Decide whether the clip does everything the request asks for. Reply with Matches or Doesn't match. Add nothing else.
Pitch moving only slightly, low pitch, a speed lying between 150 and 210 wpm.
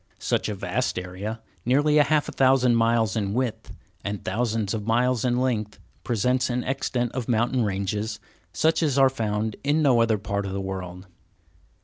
Doesn't match